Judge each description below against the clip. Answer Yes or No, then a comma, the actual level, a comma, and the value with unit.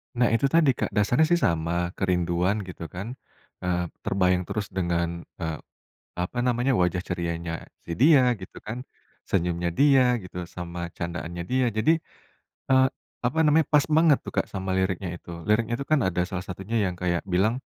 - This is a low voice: Yes, very low, 95 Hz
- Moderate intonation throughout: No, wide, 6.0 semitones